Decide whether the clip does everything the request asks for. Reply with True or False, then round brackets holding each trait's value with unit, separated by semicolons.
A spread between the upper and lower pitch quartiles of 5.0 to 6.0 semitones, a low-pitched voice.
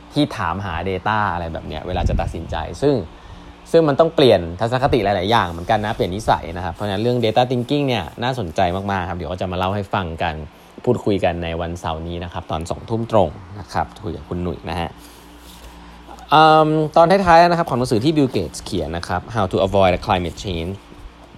True (5.4 semitones; 95 Hz)